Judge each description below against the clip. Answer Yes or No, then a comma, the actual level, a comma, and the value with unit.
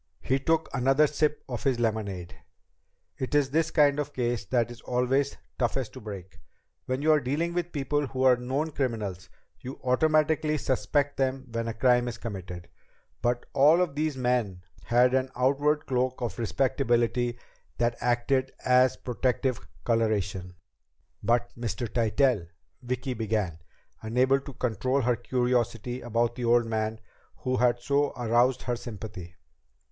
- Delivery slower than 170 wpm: Yes, average, 150 wpm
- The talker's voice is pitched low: Yes, low, 125 Hz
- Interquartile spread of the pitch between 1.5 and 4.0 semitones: Yes, average, 2.7 semitones